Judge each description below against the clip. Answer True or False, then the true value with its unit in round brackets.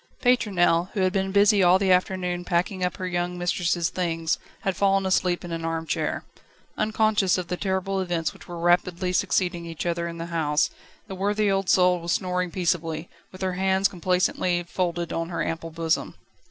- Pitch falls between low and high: True (180 Hz)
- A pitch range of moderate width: False (1.8 semitones)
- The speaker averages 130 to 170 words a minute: False (185 wpm)